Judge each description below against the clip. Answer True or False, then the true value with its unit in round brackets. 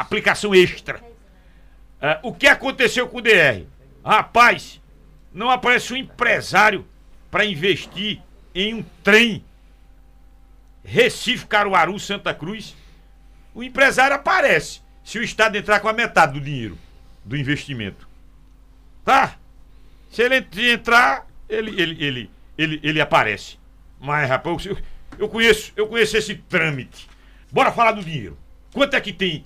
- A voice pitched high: True (205 Hz)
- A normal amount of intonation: False (7.1 semitones)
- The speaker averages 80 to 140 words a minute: True (130 wpm)